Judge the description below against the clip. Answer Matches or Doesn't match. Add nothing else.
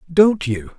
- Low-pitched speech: Doesn't match